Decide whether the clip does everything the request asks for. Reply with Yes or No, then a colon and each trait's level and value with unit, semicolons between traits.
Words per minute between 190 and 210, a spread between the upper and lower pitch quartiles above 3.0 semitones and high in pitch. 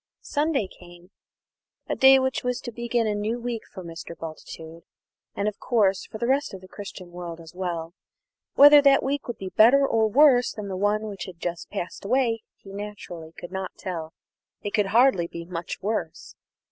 Yes: average, 195 wpm; wide, 5.4 semitones; high, 205 Hz